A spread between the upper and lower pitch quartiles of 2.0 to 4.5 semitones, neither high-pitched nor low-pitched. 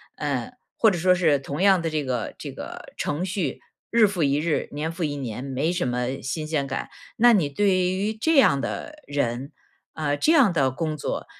No: average, 5.1 semitones; medium, 155 Hz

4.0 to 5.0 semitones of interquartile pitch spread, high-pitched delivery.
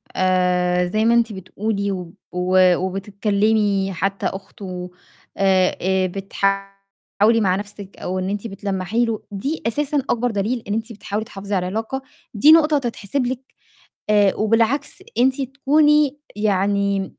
No: average, 3.4 semitones; high, 200 Hz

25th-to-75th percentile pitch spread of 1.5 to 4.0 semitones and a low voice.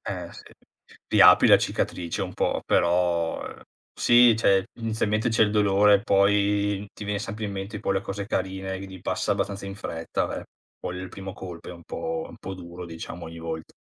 Yes: narrow, 2.6 semitones; very low, 95 Hz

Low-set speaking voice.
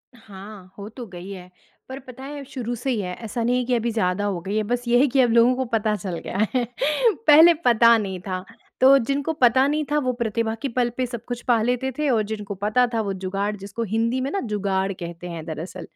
No: high, 230 Hz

